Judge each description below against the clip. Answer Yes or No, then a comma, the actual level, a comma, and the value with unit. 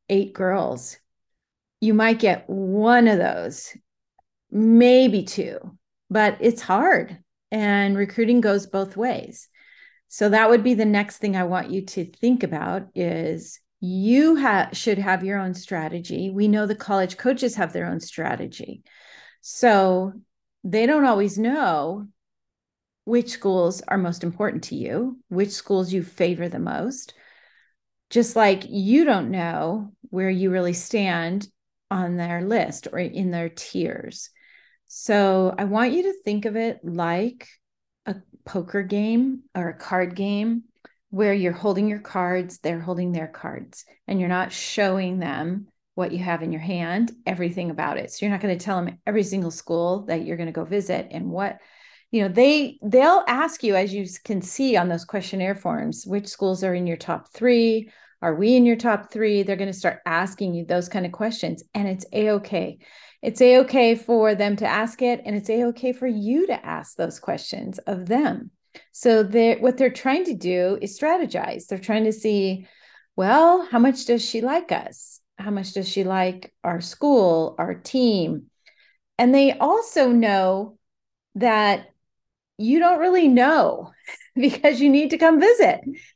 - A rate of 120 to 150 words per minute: No, average, 170 wpm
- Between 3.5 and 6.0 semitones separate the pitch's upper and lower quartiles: Yes, average, 4.2 semitones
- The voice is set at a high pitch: Yes, high, 205 Hz